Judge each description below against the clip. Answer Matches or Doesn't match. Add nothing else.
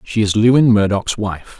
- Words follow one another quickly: Doesn't match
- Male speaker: Matches